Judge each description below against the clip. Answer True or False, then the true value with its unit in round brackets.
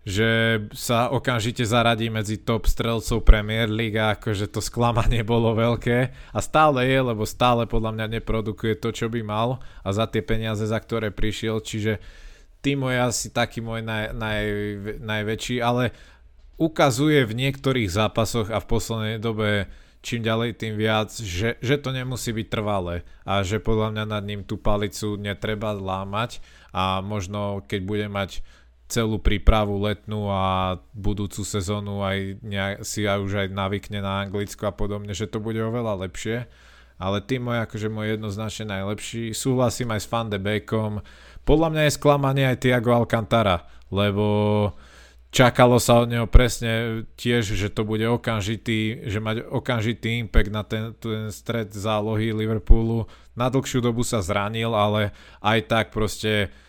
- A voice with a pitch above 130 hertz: False (110 Hz)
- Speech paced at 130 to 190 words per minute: True (160 wpm)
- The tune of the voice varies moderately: False (2.1 semitones)